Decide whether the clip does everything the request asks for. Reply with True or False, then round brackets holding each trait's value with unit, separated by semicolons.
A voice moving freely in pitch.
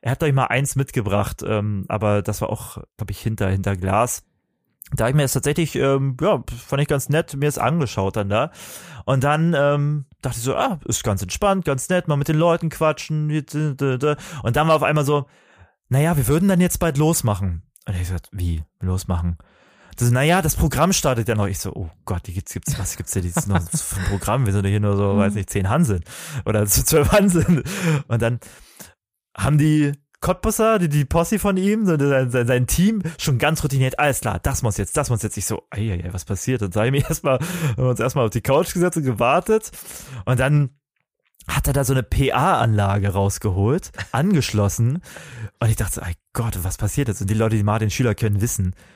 True (6.4 semitones)